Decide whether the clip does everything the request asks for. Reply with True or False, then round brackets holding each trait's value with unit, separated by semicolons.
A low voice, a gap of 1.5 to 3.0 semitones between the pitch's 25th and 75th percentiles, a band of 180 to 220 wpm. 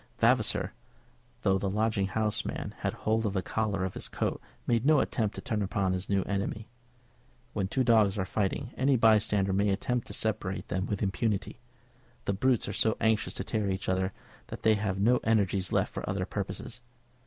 True (105 Hz; 2.5 semitones; 190 wpm)